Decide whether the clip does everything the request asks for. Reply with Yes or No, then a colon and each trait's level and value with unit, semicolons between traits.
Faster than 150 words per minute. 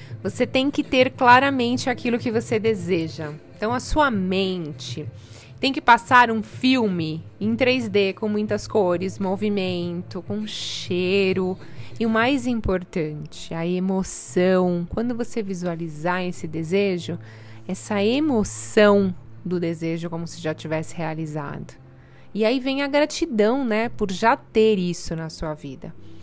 No: average, 135 wpm